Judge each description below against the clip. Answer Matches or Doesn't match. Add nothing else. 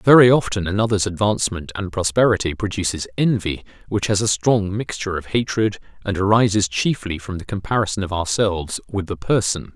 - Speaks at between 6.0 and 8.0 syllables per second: Doesn't match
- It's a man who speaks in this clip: Matches